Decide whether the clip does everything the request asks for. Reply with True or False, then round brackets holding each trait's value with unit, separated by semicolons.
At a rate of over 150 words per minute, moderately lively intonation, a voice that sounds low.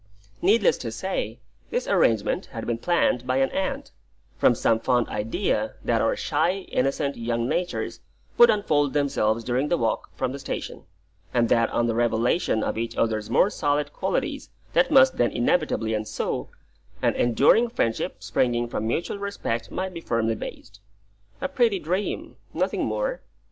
False (160 wpm; 7.9 semitones; 130 Hz)